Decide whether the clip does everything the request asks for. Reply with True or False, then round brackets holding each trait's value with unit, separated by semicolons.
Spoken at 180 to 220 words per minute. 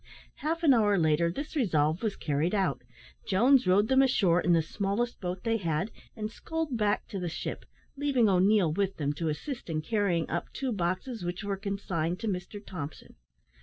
True (185 wpm)